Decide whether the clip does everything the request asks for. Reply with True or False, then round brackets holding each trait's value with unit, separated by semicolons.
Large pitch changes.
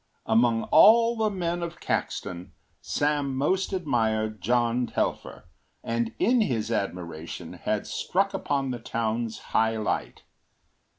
True (7.1 semitones)